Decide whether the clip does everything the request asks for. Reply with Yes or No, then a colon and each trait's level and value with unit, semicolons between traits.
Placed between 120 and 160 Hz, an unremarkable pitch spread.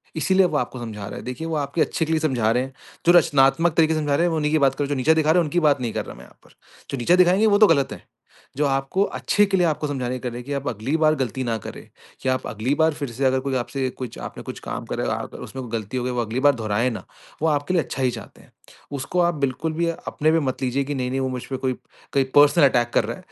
Yes: medium, 140 Hz; average, 3.8 semitones